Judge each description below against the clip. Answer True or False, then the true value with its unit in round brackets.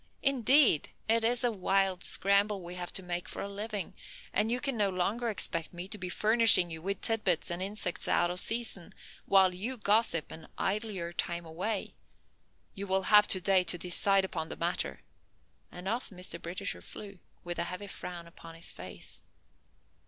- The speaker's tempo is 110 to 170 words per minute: False (185 wpm)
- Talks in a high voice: True (195 Hz)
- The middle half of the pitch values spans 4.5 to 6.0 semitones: False (3.3 semitones)